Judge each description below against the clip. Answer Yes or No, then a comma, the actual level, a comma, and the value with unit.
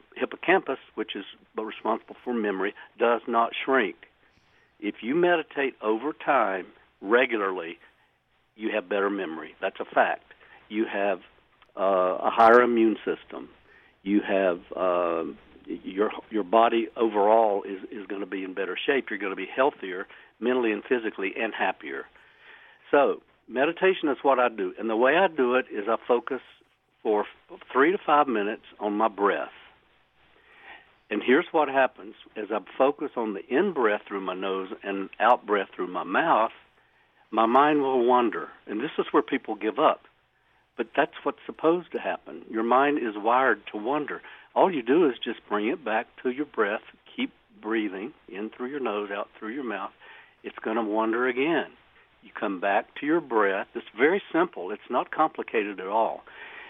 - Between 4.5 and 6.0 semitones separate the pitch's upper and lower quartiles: Yes, wide, 5.5 semitones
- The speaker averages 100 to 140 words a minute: No, average, 170 wpm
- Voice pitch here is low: Yes, low, 115 Hz